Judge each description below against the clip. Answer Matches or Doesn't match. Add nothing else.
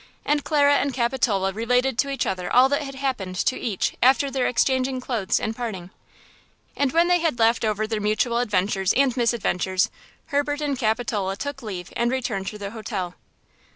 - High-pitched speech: Matches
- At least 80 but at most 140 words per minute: Doesn't match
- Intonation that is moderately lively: Matches